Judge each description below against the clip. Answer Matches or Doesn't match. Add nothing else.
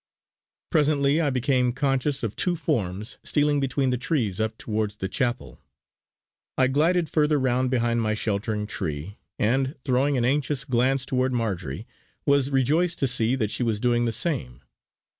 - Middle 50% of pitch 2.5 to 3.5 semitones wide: Doesn't match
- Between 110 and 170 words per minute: Matches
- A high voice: Doesn't match